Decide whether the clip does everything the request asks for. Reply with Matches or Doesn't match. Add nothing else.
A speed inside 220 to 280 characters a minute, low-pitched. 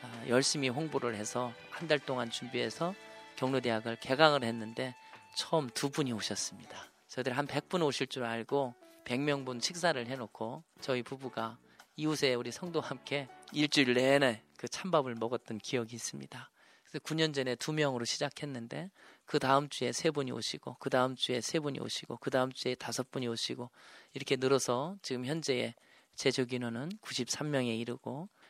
Doesn't match